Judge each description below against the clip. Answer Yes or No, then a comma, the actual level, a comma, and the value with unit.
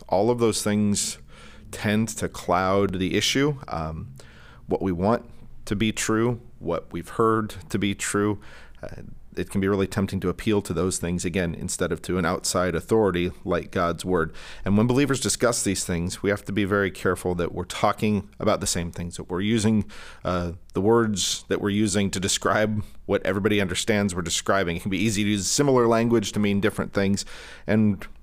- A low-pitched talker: Yes, low, 100 Hz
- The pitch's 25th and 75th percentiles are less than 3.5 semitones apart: Yes, average, 2.8 semitones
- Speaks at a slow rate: No, average, 195 wpm